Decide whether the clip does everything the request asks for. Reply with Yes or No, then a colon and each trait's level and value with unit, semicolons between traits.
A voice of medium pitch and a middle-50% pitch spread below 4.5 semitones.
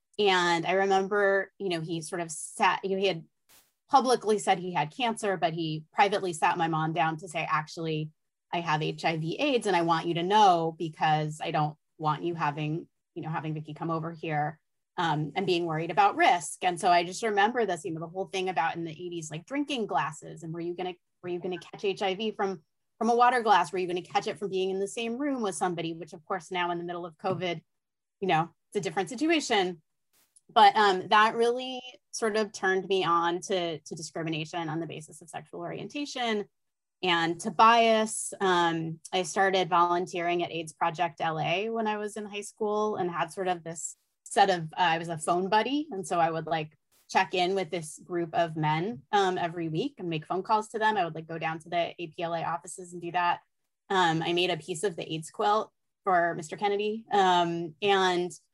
Yes: medium, 180 Hz; average, 3.3 semitones